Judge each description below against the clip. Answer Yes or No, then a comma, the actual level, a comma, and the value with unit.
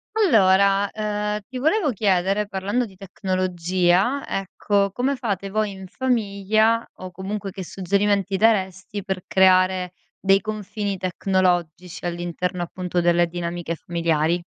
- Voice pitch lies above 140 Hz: Yes, high, 190 Hz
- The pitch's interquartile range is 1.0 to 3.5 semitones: Yes, narrow, 2.5 semitones